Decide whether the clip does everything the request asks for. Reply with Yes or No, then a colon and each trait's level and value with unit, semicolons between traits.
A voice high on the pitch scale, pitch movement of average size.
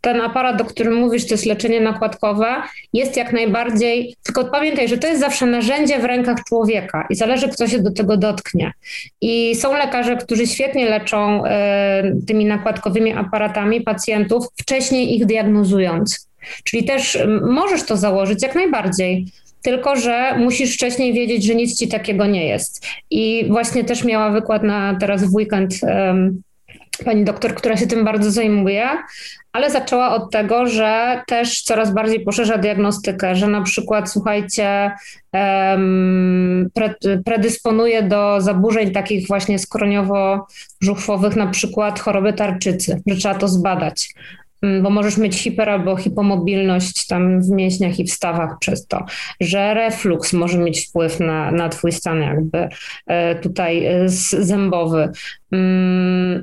Yes: high, 210 Hz; average, 3.1 semitones